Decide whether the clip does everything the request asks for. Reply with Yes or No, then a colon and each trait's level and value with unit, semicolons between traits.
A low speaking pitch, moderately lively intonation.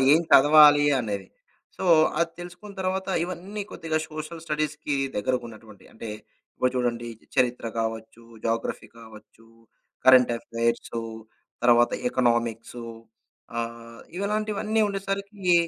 No: low, 130 Hz; wide, 7.1 semitones